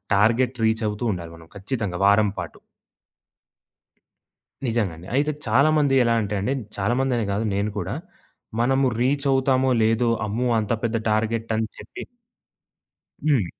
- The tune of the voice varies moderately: Yes, average, 3.8 semitones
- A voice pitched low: Yes, low, 115 Hz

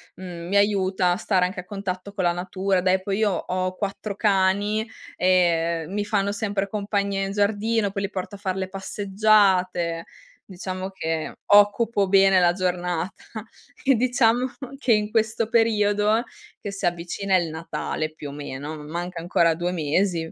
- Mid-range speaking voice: No, high, 195 Hz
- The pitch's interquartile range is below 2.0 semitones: No, narrow, 2.5 semitones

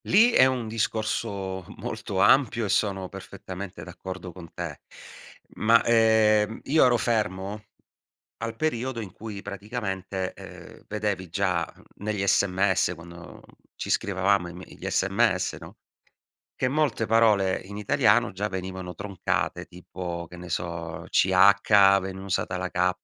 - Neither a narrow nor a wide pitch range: Yes, average, 3.0 semitones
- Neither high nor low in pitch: No, low, 100 Hz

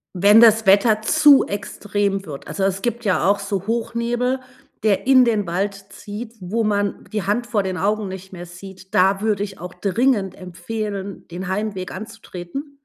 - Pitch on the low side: No, high, 205 Hz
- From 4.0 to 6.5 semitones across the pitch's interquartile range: No, narrow, 2.6 semitones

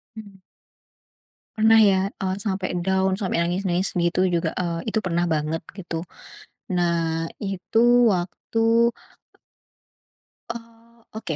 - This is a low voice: No, high, 190 Hz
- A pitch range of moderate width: Yes, average, 4.1 semitones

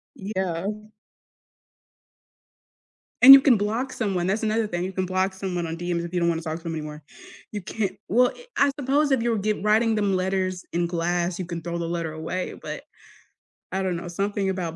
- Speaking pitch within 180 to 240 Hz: Yes, medium, 185 Hz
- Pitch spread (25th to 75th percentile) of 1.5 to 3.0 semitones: No, average, 3.6 semitones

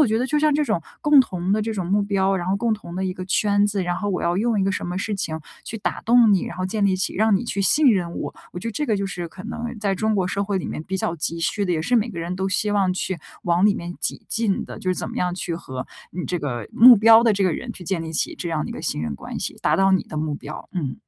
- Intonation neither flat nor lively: Yes, average, 3.5 semitones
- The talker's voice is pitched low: No, high, 190 Hz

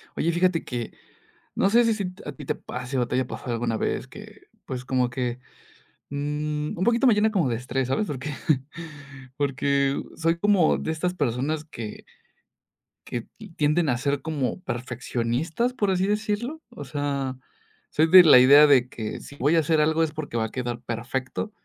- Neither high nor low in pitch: Yes, medium, 145 Hz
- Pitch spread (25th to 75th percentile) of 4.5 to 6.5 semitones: Yes, average, 5.1 semitones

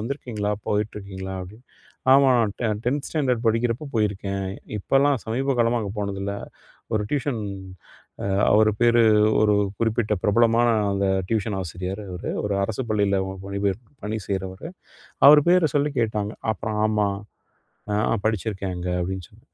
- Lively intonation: No, average, 3.3 semitones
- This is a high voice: No, low, 110 Hz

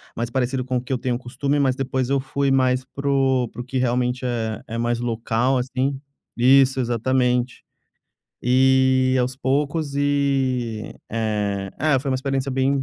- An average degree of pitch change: No, narrow, 1.7 semitones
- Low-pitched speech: Yes, low, 130 Hz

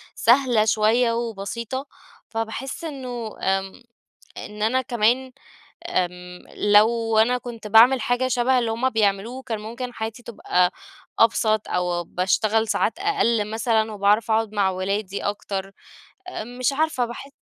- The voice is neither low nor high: No, high, 225 Hz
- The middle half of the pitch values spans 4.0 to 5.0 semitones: No, average, 2.9 semitones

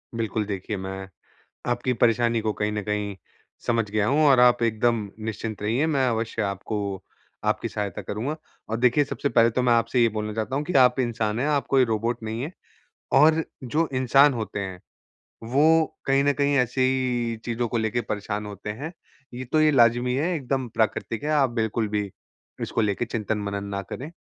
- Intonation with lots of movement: No, average, 3.6 semitones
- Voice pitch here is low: Yes, low, 115 Hz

